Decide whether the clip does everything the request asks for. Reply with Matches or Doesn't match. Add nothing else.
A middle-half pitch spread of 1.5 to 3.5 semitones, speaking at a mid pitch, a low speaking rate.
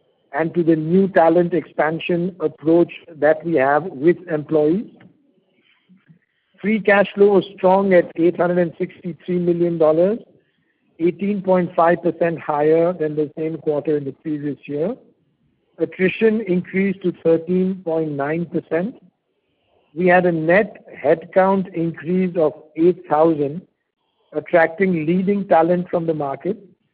Matches